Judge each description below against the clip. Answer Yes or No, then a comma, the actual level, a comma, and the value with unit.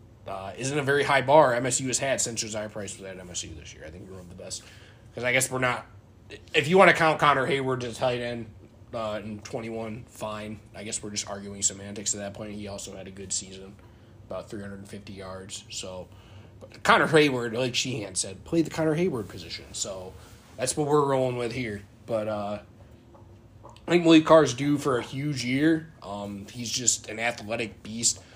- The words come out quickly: Yes, fast, 215 wpm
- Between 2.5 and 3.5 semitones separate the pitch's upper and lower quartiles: No, average, 4.0 semitones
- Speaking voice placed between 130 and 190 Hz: No, low, 110 Hz